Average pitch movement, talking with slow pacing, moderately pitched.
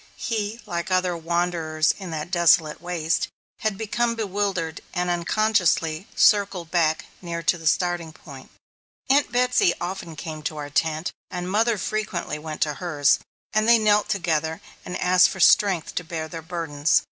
No: average, 3.7 semitones; average, 160 wpm; medium, 175 Hz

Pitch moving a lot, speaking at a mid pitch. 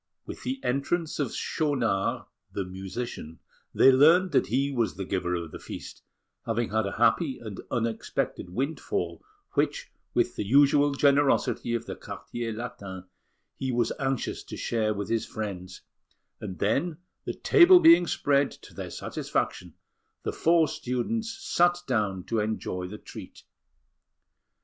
No: wide, 6.1 semitones; low, 120 Hz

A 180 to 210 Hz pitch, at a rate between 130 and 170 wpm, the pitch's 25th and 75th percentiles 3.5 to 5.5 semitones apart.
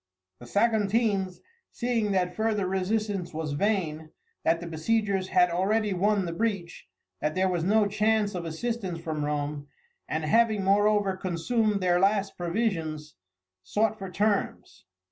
Yes: high, 190 Hz; average, 140 wpm; average, 4.0 semitones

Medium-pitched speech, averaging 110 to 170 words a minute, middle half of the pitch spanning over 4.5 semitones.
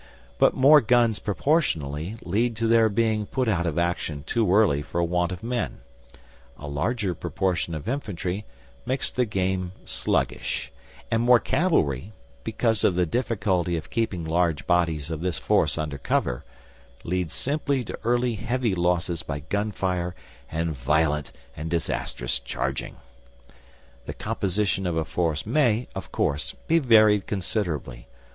No: very low, 95 Hz; average, 140 wpm; wide, 5.6 semitones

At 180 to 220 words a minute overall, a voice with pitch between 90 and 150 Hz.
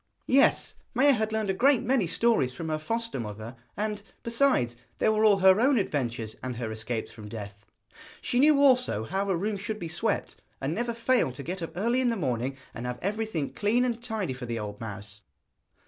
No: fast, 205 wpm; high, 190 Hz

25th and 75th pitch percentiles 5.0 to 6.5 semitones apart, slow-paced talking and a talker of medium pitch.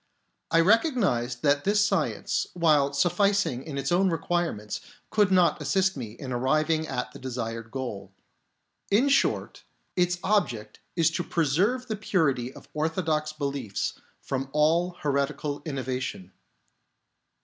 Yes: wide, 5.4 semitones; slow, 125 wpm; medium, 155 Hz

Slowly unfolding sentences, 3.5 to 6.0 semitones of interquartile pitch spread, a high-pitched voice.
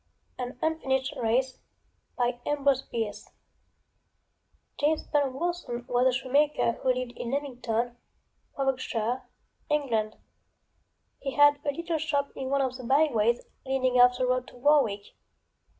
No: slow, 120 wpm; average, 2.8 semitones; very high, 260 Hz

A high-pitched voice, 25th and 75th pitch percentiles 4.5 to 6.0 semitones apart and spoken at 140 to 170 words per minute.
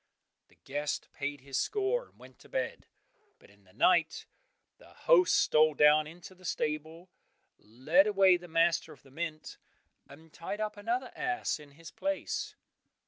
No: medium, 165 Hz; average, 5.3 semitones; average, 160 wpm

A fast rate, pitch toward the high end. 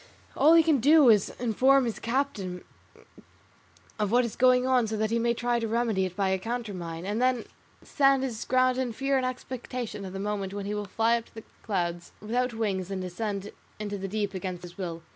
Yes: fast, 220 wpm; high, 225 Hz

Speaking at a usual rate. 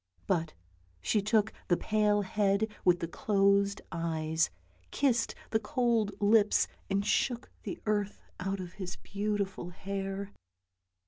No: slow, 125 wpm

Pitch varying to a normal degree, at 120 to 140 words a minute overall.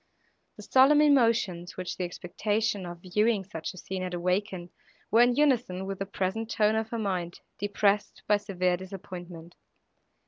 No: average, 3.4 semitones; average, 160 wpm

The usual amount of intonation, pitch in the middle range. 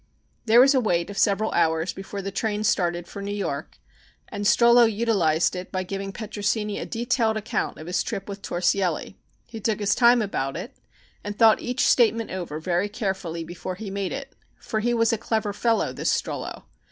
No: average, 3.6 semitones; high, 205 Hz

